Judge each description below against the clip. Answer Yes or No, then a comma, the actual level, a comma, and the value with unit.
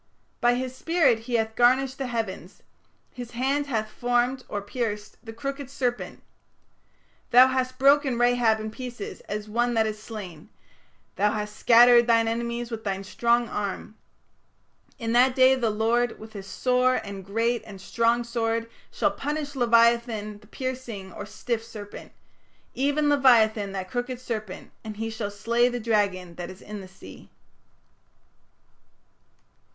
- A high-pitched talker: Yes, high, 235 Hz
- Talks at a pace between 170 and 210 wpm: No, average, 150 wpm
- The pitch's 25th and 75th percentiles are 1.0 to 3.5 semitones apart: Yes, average, 2.8 semitones